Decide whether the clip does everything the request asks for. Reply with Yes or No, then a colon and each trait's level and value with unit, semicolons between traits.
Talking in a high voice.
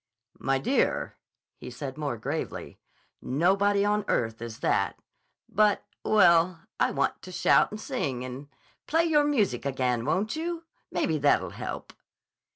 No: medium, 170 Hz